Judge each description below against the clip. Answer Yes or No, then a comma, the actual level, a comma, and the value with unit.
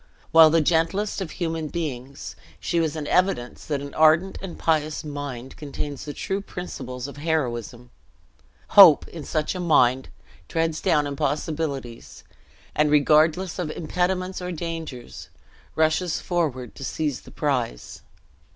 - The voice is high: No, medium, 155 Hz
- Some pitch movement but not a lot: Yes, average, 3.0 semitones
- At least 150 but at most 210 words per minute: No, slow, 135 wpm